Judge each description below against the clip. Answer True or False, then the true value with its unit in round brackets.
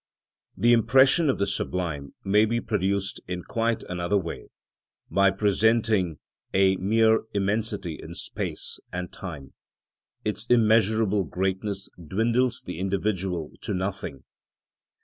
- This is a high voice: False (100 Hz)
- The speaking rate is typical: False (115 wpm)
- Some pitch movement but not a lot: True (3.4 semitones)